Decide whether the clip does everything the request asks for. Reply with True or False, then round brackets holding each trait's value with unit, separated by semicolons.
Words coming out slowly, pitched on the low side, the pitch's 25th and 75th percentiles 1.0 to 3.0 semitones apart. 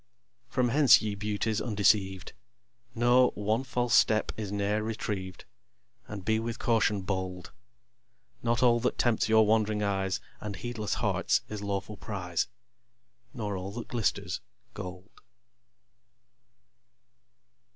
True (120 wpm; 105 Hz; 2.6 semitones)